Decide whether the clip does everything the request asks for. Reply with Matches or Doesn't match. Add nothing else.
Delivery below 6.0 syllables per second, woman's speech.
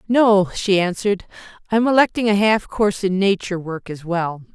Matches